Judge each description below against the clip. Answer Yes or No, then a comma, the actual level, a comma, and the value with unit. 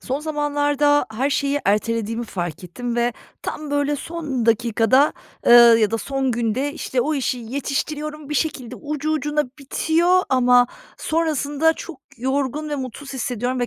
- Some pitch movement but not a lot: Yes, average, 3.6 semitones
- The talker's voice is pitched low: No, very high, 275 Hz